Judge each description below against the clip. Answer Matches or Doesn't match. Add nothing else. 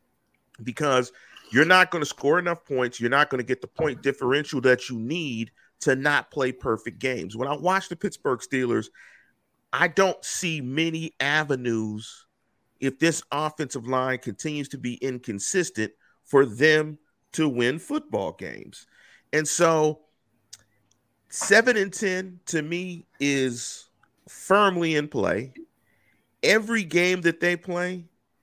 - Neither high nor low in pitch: Matches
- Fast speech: Doesn't match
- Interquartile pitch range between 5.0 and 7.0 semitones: Matches